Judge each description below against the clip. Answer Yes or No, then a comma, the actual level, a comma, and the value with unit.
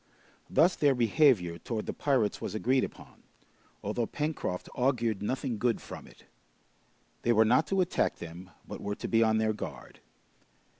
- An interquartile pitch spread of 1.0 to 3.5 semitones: No, average, 4.1 semitones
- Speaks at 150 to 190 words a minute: Yes, average, 160 wpm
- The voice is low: Yes, low, 115 Hz